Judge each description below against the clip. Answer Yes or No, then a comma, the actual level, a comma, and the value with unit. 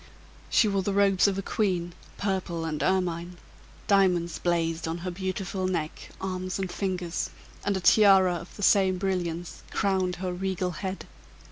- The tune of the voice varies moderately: No, narrow, 1.8 semitones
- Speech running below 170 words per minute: Yes, average, 155 wpm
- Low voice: No, medium, 185 Hz